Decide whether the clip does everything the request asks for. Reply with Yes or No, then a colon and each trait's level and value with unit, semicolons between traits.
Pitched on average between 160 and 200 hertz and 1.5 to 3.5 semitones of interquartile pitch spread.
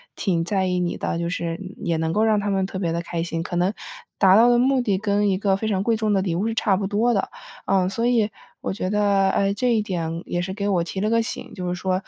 Yes: high, 195 Hz; average, 2.9 semitones